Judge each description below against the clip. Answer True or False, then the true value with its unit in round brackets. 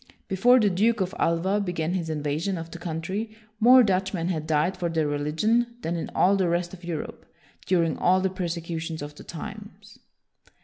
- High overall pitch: False (175 Hz)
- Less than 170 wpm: False (185 wpm)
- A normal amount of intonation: True (3.3 semitones)